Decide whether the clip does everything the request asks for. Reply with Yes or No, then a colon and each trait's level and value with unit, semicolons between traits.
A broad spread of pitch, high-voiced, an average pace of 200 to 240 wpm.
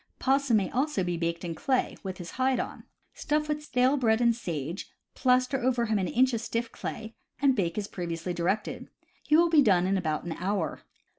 Yes: wide, 6.5 semitones; high, 220 Hz; fast, 205 wpm